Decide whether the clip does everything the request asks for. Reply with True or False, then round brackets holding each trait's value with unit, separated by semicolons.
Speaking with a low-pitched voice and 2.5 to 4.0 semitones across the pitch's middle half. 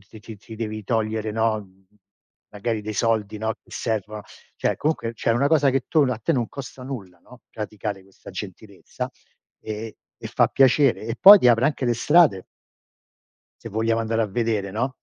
True (115 Hz; 2.8 semitones)